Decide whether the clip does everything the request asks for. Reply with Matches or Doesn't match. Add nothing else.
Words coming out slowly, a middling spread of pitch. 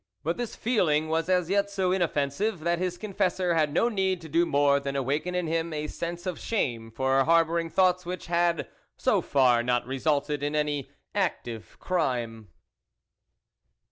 Doesn't match